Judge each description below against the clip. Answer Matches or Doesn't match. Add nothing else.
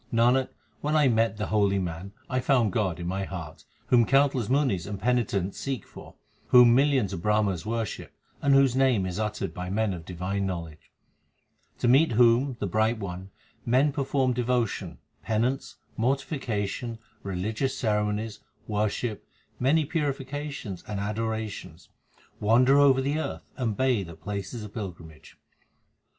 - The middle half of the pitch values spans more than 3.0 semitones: Matches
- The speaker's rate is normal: Matches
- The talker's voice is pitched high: Doesn't match